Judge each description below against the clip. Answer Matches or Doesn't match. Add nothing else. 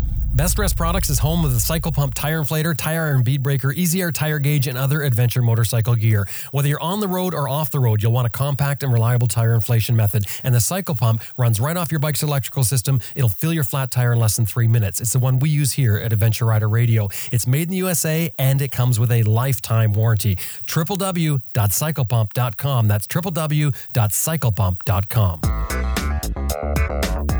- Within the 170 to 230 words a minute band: Matches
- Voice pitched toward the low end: Matches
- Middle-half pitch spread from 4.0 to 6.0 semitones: Matches